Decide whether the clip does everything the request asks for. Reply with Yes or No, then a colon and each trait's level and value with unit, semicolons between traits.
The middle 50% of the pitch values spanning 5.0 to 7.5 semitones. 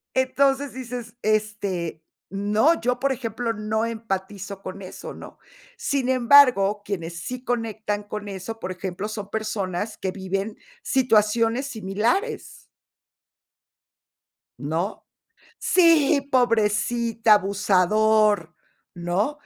No: average, 3.7 semitones